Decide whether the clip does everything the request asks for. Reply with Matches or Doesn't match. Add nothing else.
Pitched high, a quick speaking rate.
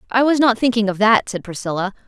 Matches